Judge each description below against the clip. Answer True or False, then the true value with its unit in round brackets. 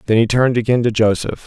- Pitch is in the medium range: False (115 Hz)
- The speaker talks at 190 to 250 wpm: True (245 wpm)